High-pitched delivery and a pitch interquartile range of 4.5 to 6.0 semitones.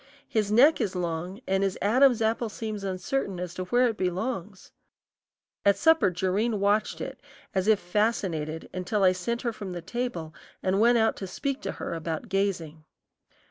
No: high, 200 Hz; average, 3.7 semitones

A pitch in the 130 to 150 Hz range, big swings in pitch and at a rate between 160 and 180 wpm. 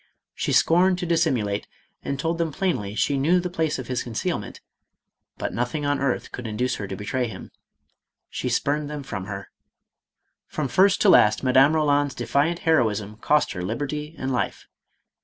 Yes: medium, 140 Hz; wide, 5.8 semitones; average, 170 wpm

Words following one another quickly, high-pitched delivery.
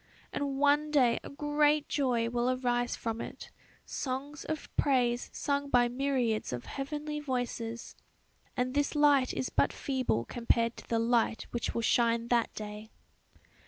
No: average, 150 wpm; very high, 255 Hz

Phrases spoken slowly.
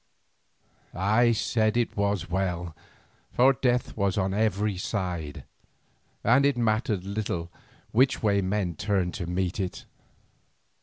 Yes: slow, 130 wpm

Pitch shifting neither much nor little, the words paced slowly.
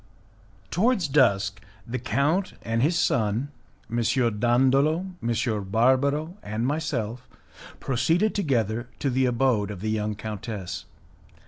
Yes: average, 4.6 semitones; slow, 115 wpm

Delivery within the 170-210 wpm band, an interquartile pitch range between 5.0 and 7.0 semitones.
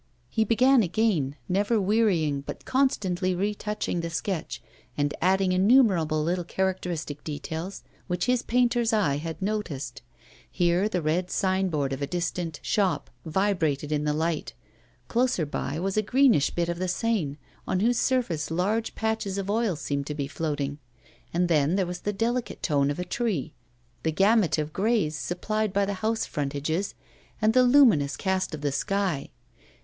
No: average, 160 wpm; wide, 5.6 semitones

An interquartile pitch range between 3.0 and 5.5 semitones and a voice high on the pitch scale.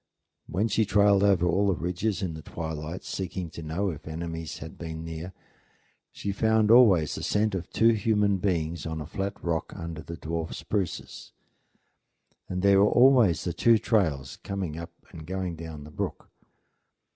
No: average, 3.9 semitones; very low, 90 Hz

